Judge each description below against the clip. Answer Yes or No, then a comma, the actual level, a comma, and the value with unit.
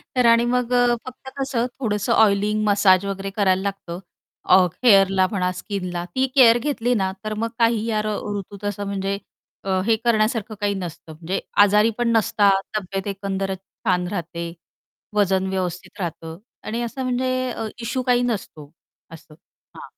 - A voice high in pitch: Yes, high, 205 Hz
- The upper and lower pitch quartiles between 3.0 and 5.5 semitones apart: Yes, average, 3.5 semitones